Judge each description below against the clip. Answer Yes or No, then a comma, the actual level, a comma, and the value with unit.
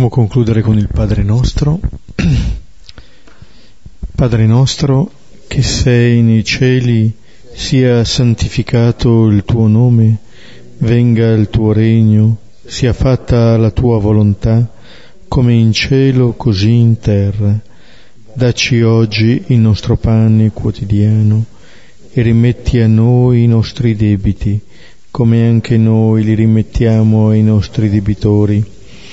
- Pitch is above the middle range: No, low, 115 Hz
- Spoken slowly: Yes, slow, 105 wpm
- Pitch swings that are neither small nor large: No, narrow, 1.7 semitones